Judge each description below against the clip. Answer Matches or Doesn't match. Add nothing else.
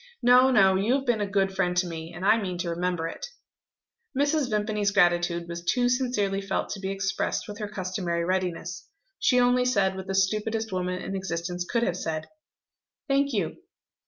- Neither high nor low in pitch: Doesn't match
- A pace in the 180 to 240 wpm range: Matches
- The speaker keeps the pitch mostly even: Doesn't match